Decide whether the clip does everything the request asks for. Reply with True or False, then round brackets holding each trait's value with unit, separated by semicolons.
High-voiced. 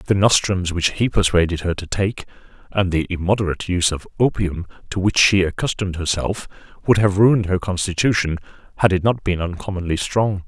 False (95 Hz)